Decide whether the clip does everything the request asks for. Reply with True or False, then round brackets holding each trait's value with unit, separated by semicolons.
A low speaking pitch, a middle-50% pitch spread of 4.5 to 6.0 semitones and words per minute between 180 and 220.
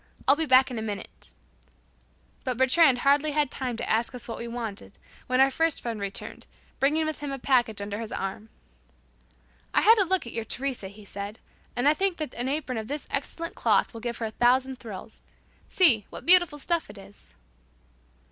False (255 Hz; 4.8 semitones; 200 wpm)